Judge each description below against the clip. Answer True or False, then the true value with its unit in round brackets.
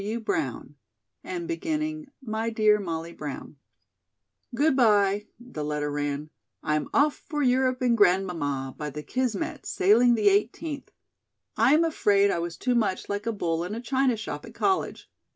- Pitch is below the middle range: False (215 Hz)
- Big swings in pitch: True (7.1 semitones)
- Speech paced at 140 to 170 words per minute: True (165 wpm)